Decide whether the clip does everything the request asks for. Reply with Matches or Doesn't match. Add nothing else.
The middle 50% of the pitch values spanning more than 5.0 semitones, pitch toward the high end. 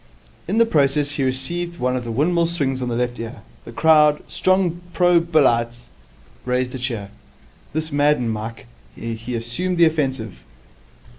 Doesn't match